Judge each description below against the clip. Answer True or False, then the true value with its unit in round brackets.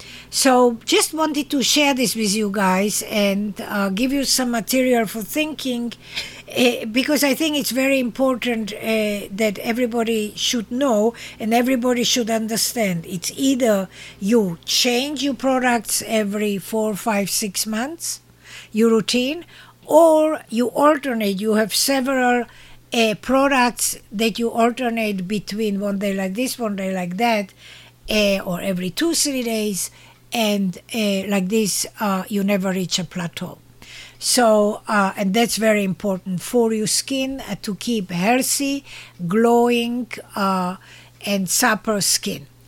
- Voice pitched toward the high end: True (225 Hz)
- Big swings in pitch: False (3.7 semitones)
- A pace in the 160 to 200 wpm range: False (140 wpm)